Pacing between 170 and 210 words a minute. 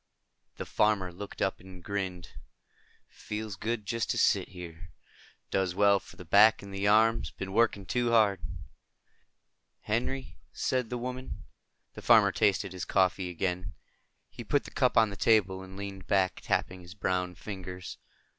No: average, 155 wpm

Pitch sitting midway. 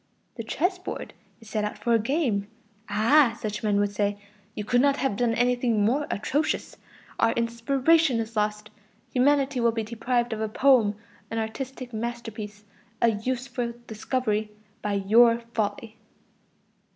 No: high, 230 Hz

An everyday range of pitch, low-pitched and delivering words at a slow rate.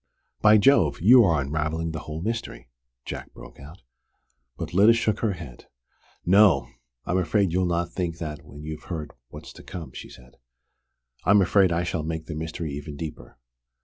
No: average, 3.8 semitones; very low, 85 Hz; average, 175 wpm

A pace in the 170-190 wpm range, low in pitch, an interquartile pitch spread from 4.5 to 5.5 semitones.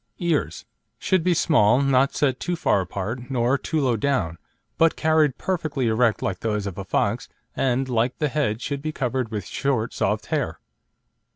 Yes: average, 175 wpm; low, 130 Hz; average, 5.0 semitones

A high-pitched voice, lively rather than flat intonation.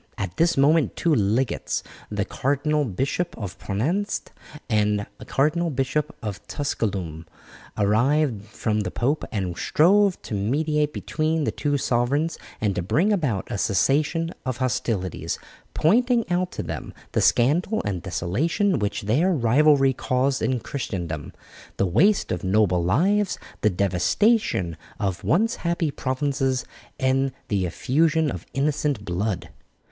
No: low, 135 Hz; wide, 7.3 semitones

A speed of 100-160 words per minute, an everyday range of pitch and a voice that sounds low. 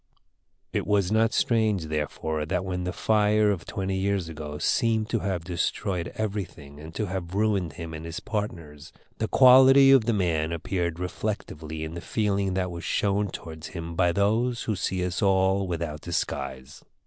No: average, 170 wpm; average, 4.1 semitones; very low, 95 Hz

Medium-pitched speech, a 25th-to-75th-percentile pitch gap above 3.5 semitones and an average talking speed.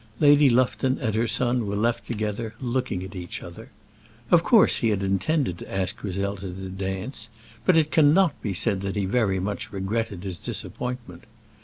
No: low, 110 Hz; average, 4.7 semitones; average, 175 wpm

